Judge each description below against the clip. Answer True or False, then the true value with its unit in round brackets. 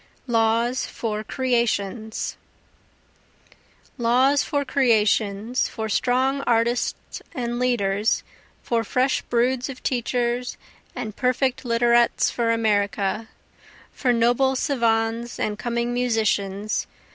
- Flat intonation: True (2.2 semitones)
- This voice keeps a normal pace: False (95 wpm)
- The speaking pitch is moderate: False (235 Hz)